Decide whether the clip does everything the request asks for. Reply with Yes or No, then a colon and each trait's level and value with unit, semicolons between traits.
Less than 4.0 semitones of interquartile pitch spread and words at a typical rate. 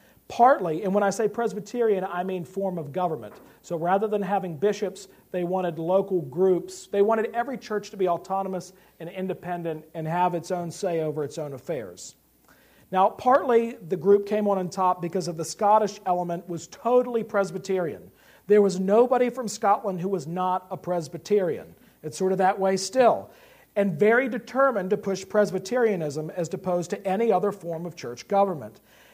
Yes: average, 2.8 semitones; average, 175 wpm